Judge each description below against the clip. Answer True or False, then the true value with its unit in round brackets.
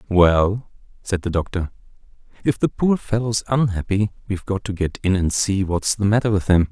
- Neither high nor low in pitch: False (100 Hz)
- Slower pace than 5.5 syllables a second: True (5.2 syllables/s)